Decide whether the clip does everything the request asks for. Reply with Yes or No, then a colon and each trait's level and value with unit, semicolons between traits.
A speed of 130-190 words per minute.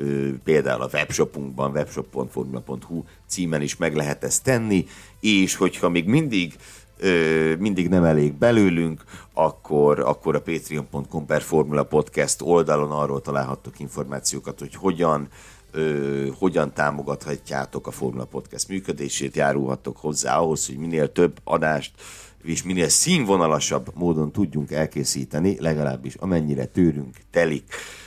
No: average, 115 wpm